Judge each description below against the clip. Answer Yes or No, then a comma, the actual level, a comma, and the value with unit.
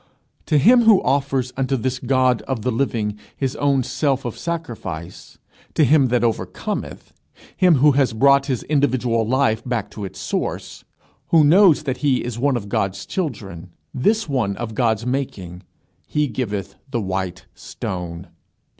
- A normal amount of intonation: Yes, average, 4.4 semitones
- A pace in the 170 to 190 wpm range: No, average, 160 wpm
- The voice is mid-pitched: No, low, 125 Hz